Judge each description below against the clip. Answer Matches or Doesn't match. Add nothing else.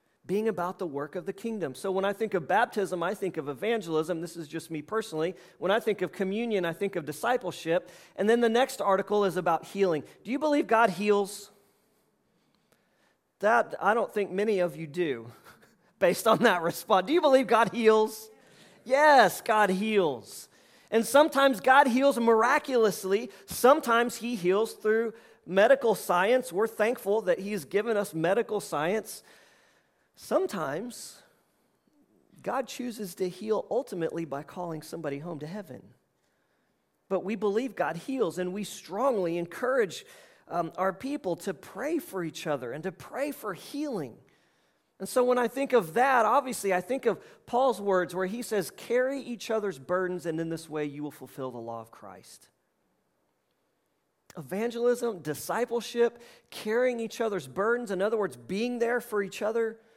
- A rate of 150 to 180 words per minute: Matches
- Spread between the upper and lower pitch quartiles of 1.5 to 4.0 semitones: Doesn't match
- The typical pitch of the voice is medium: Doesn't match